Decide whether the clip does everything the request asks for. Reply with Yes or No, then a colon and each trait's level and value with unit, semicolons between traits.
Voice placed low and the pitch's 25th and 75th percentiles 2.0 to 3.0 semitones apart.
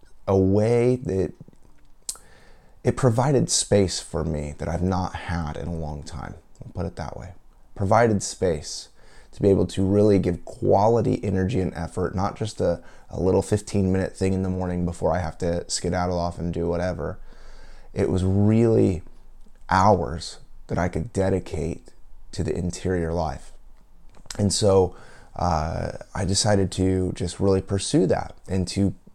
Yes: very low, 95 Hz; narrow, 2.4 semitones